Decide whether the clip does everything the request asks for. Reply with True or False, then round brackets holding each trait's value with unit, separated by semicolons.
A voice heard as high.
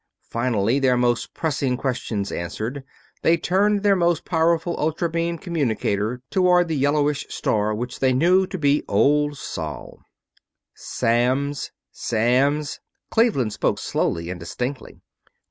False (140 Hz)